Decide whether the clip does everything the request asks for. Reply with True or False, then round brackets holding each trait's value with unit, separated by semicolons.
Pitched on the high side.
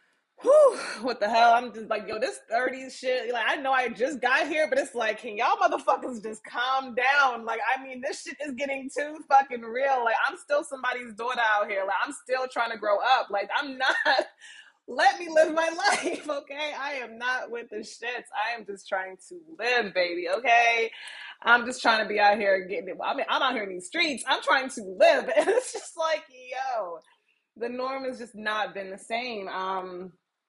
True (250 Hz)